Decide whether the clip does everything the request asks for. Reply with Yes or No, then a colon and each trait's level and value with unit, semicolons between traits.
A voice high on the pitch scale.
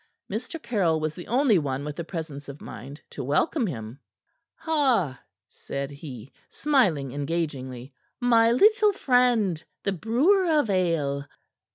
No: medium, 170 Hz